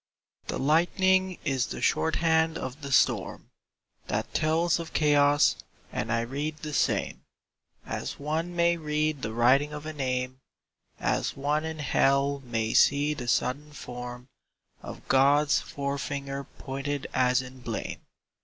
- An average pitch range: Yes, average, 3.0 semitones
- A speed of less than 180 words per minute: Yes, average, 140 wpm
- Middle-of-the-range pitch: Yes, medium, 145 Hz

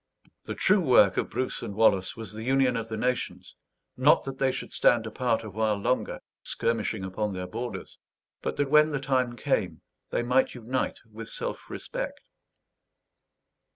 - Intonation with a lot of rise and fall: No, average, 3.2 semitones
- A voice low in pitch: Yes, low, 120 Hz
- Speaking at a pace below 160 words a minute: No, average, 165 wpm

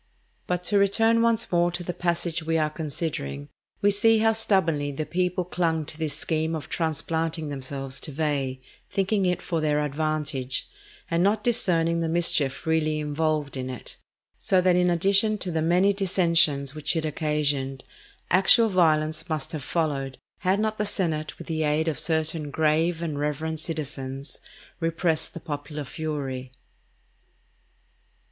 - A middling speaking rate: Yes, average, 155 wpm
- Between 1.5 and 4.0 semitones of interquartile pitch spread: Yes, average, 3.2 semitones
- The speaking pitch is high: No, medium, 160 Hz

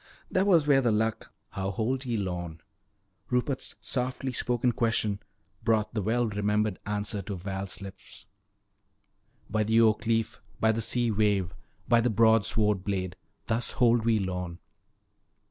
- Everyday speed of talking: Yes, average, 145 wpm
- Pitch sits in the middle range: No, low, 110 Hz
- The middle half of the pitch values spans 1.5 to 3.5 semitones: Yes, average, 2.9 semitones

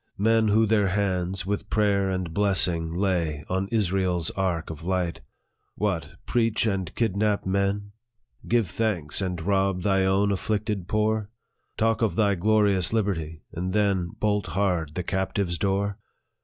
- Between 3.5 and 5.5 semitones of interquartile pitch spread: No, narrow, 2.4 semitones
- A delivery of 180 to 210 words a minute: No, average, 145 wpm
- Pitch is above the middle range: No, very low, 95 Hz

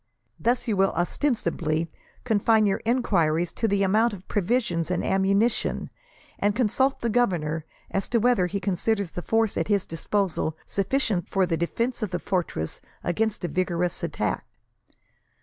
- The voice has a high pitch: Yes, high, 195 Hz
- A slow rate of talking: No, average, 150 wpm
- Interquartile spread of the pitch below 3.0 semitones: No, average, 4.3 semitones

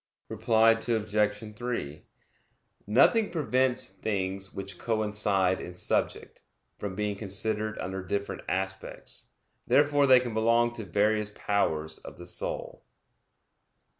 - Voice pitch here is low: Yes, low, 105 Hz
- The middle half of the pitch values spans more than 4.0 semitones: No, average, 2.9 semitones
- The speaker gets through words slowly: Yes, slow, 110 wpm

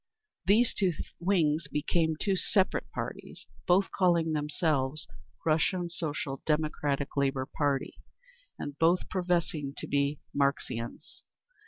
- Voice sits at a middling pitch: Yes, medium, 155 Hz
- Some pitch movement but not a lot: Yes, average, 3.8 semitones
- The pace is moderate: No, slow, 110 wpm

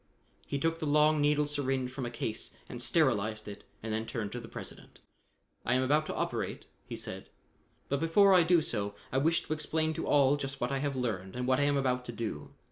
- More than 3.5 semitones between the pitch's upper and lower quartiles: Yes, average, 4.0 semitones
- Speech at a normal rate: No, fast, 225 wpm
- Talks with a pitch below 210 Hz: Yes, low, 135 Hz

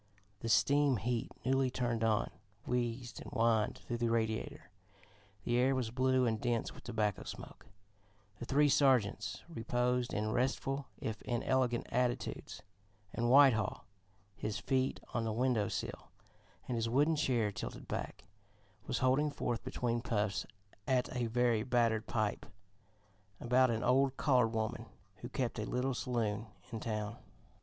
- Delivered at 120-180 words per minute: Yes, average, 145 wpm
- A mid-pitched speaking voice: No, low, 120 Hz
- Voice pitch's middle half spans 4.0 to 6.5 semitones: No, narrow, 2.5 semitones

